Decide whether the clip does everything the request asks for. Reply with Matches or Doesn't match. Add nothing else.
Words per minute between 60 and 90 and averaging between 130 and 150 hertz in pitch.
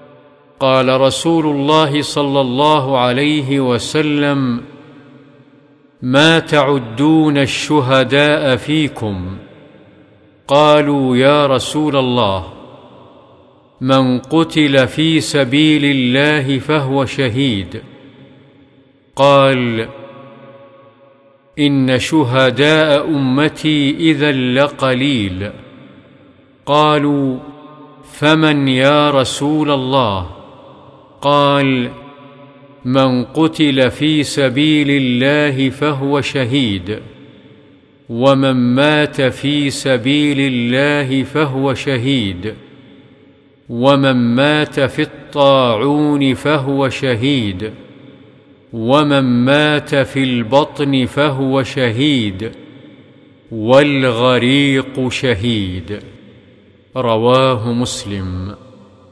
Matches